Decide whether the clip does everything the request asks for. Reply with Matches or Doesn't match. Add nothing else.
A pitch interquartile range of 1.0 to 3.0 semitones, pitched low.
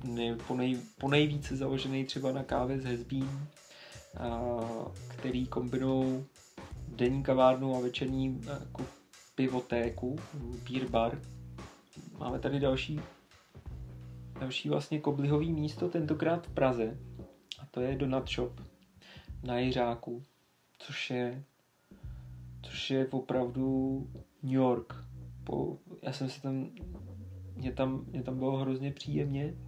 Matches